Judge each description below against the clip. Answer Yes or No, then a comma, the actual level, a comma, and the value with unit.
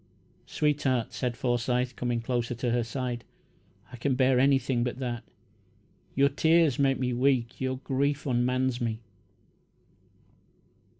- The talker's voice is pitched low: Yes, low, 125 Hz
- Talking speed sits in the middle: No, slow, 125 wpm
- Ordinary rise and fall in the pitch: No, narrow, 1.9 semitones